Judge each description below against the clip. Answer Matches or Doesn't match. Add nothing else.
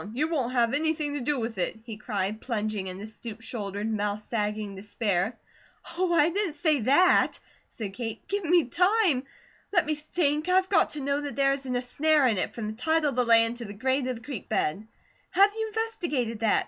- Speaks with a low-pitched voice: Doesn't match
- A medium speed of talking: Doesn't match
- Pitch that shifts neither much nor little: Doesn't match